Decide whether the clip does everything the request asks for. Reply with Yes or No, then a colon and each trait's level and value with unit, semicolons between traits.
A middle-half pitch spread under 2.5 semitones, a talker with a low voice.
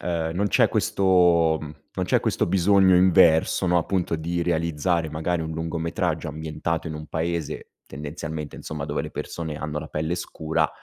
Yes: narrow, 1.9 semitones; very low, 80 Hz